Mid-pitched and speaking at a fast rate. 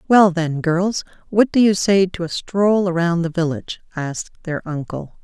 No: medium, 180 Hz; average, 185 wpm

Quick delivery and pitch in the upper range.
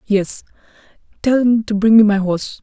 No: average, 185 wpm; high, 210 Hz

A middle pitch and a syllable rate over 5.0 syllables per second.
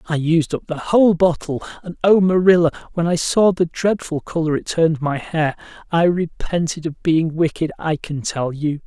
No: medium, 165 Hz; 4.9 syllables/s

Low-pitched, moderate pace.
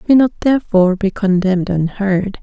No: high, 200 Hz; average, 175 wpm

